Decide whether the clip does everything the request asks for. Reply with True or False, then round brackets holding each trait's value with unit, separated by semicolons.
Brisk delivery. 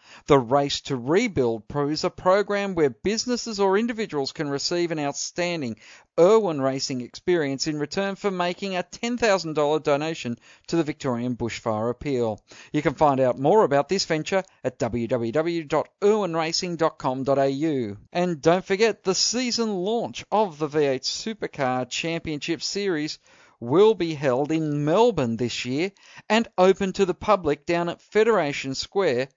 False (140 wpm)